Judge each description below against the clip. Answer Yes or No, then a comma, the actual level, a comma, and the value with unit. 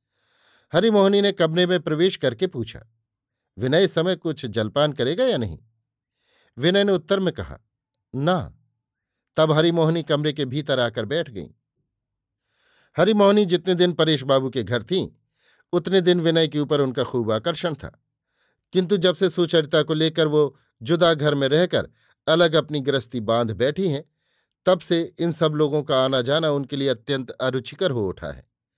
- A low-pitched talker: No, medium, 150 Hz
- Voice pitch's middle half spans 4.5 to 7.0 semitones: Yes, wide, 5.5 semitones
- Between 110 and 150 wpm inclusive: No, average, 160 wpm